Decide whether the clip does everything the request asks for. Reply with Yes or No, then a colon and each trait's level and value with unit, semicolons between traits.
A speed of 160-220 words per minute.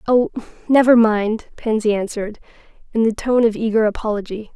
No: average, 145 wpm